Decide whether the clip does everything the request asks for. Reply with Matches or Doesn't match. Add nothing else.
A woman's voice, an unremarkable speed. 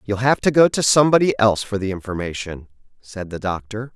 Doesn't match